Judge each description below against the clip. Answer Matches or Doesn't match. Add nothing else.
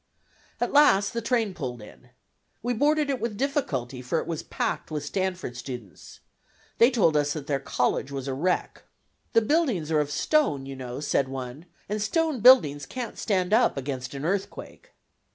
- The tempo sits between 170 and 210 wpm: Matches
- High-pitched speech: Doesn't match